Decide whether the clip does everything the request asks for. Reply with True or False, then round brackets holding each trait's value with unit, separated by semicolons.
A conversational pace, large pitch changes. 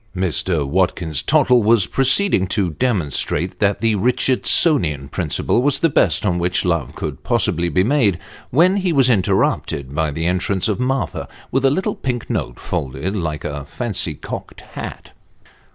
True (160 wpm; 7.6 semitones)